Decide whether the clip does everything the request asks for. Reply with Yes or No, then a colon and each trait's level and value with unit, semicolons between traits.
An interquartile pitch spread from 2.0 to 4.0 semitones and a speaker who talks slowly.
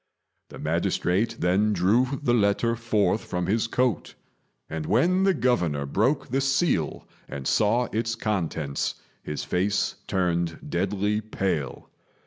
No: average, 5.1 semitones; slow, 125 wpm